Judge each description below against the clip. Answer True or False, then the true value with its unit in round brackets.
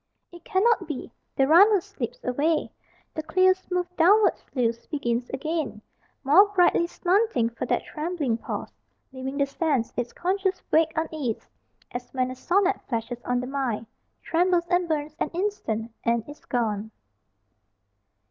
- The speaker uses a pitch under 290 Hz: False (305 Hz)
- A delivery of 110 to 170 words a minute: True (145 wpm)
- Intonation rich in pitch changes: True (6.4 semitones)